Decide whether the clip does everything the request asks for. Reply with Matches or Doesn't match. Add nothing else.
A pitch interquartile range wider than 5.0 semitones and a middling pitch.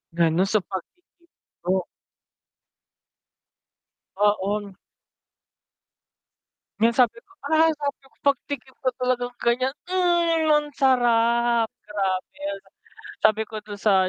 Doesn't match